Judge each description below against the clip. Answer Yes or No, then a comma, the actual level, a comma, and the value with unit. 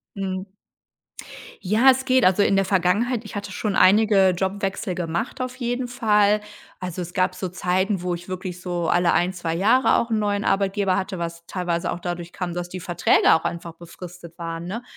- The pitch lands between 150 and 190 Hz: Yes, medium, 185 Hz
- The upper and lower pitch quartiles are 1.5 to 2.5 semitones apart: No, average, 2.9 semitones